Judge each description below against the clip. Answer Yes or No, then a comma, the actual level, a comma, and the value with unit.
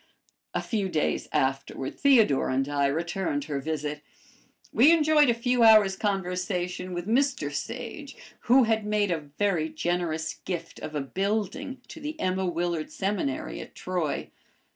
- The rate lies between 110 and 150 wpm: Yes, average, 145 wpm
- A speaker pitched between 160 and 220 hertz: Yes, medium, 185 Hz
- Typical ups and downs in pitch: No, wide, 6.3 semitones